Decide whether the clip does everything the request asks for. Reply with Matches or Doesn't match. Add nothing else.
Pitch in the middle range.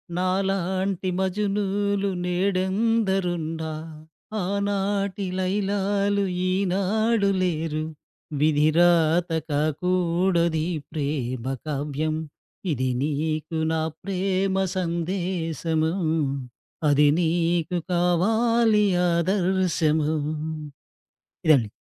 Matches